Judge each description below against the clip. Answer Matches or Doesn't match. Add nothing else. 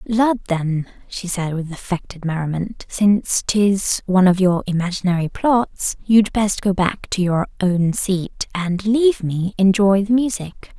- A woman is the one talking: Matches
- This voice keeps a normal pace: Matches